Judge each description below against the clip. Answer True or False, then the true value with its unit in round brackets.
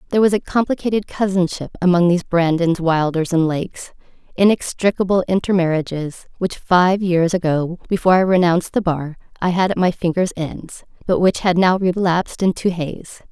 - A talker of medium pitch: True (180 Hz)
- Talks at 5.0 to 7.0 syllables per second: True (5.3 syllables/s)